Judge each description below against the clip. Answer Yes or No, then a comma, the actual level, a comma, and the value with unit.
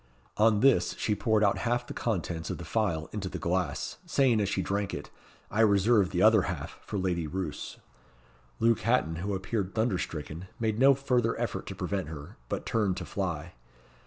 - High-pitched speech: No, low, 100 Hz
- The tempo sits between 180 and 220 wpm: Yes, average, 190 wpm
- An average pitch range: Yes, average, 4.0 semitones